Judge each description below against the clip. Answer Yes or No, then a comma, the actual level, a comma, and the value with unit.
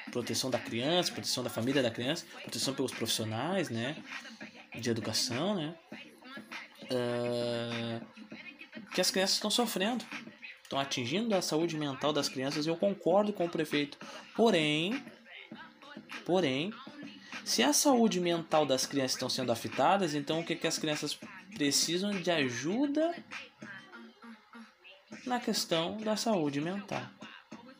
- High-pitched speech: No, medium, 170 Hz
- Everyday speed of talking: Yes, average, 130 wpm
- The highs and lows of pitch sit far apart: Yes, wide, 8.2 semitones